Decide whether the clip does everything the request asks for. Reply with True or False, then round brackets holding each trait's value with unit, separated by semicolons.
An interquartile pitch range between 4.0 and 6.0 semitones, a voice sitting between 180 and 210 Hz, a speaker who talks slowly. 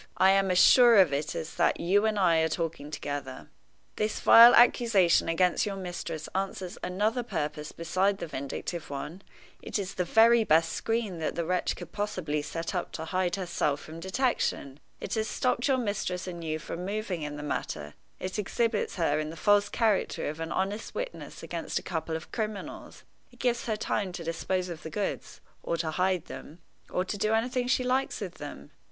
False (4.7 semitones; 185 Hz; 195 wpm)